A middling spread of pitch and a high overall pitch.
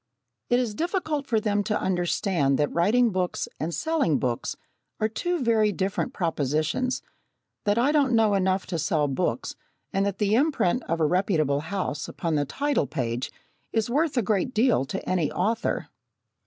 No: wide, 6.7 semitones; high, 200 Hz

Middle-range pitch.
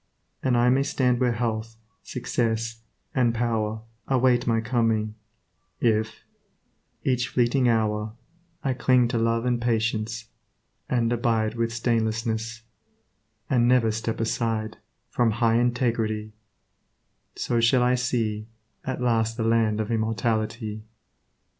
No: low, 115 Hz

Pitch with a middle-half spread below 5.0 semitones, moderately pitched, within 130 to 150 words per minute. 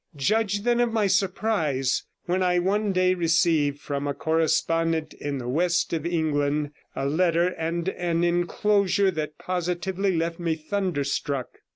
Yes: average, 3.4 semitones; medium, 170 Hz; average, 145 wpm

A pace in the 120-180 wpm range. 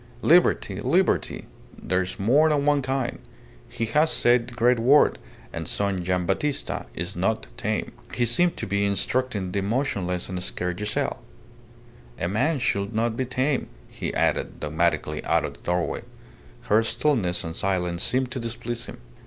Yes: average, 160 wpm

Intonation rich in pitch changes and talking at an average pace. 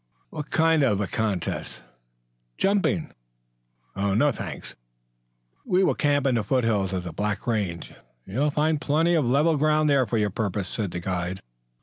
Yes: wide, 8.0 semitones; average, 165 wpm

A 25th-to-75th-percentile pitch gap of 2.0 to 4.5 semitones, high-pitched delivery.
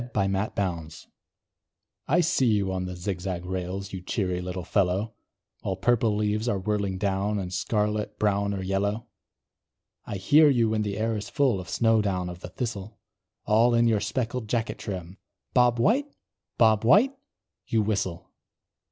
No: average, 3.2 semitones; low, 105 Hz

